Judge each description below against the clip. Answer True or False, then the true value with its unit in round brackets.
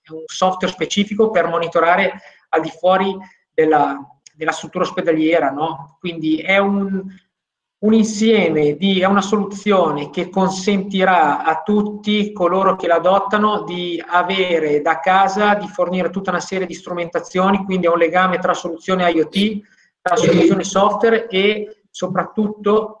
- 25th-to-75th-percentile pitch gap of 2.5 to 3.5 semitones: True (3.0 semitones)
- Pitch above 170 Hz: True (185 Hz)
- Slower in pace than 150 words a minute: True (135 wpm)